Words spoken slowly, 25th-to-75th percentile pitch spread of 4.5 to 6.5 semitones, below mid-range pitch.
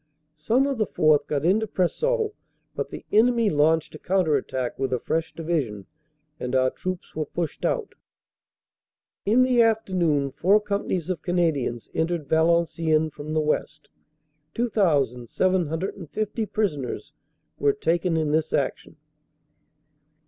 No: slow, 125 wpm; wide, 5.4 semitones; medium, 165 Hz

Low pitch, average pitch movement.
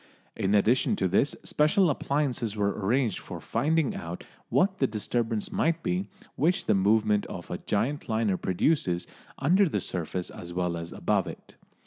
No: low, 115 Hz; wide, 7.6 semitones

